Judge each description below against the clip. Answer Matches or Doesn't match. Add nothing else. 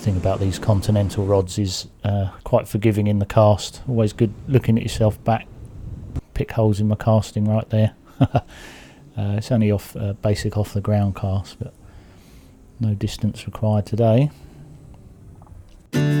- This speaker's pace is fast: Doesn't match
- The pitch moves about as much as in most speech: Doesn't match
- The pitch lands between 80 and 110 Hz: Matches